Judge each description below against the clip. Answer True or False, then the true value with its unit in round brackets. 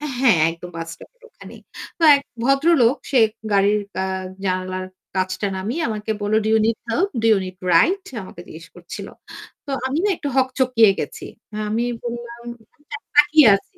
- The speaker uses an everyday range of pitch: False (6.5 semitones)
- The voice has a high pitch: True (225 Hz)